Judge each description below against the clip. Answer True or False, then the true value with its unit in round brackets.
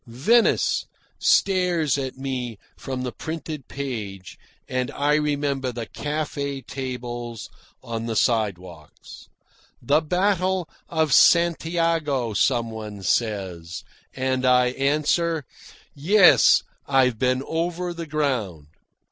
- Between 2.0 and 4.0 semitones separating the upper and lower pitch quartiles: False (5.0 semitones)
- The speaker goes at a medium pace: False (105 wpm)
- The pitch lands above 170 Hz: False (135 Hz)